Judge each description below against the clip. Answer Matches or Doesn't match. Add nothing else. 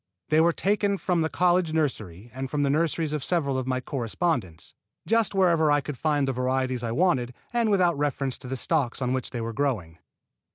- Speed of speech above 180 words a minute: Matches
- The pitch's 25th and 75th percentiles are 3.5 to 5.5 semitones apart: Matches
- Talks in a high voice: Doesn't match